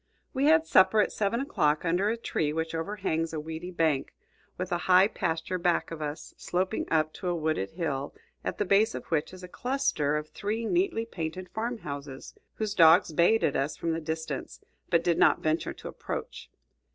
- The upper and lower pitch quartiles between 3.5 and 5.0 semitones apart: Yes, average, 4.6 semitones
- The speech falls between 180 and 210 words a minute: Yes, average, 195 wpm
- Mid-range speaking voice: Yes, medium, 170 Hz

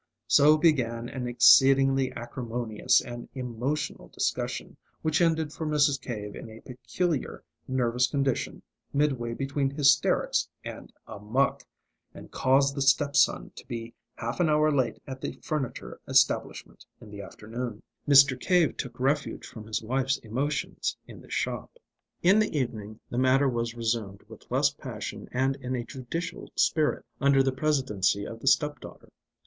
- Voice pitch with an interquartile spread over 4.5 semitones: No, average, 3.3 semitones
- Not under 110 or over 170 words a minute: Yes, average, 150 wpm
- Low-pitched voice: Yes, low, 130 Hz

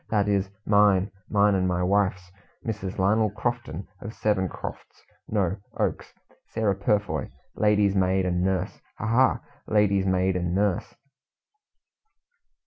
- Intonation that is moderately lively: No, narrow, 2.0 semitones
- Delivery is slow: Yes, slow, 130 wpm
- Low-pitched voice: Yes, low, 100 Hz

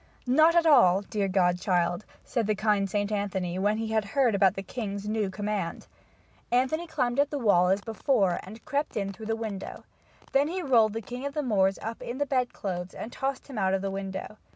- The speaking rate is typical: No, fast, 215 wpm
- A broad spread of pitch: No, average, 4.5 semitones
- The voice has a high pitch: Yes, high, 215 Hz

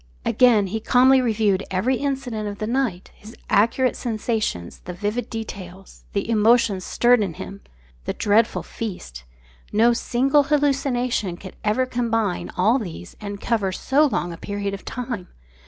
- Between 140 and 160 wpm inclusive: Yes, average, 150 wpm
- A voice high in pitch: Yes, high, 220 Hz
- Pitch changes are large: No, average, 3.8 semitones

